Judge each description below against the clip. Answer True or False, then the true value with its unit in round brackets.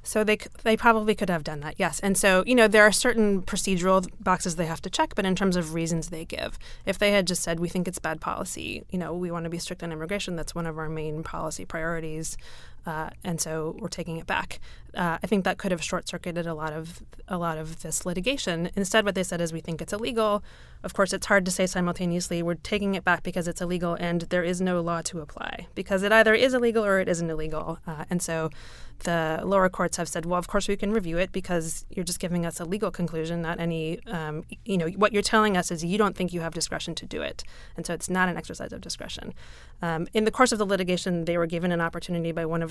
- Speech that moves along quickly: True (255 wpm)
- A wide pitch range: False (2.8 semitones)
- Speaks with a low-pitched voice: False (180 Hz)